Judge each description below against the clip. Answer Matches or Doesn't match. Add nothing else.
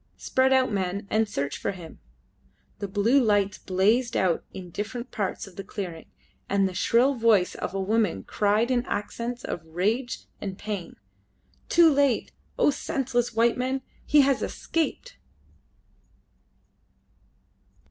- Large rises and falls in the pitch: Doesn't match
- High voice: Matches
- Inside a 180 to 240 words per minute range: Doesn't match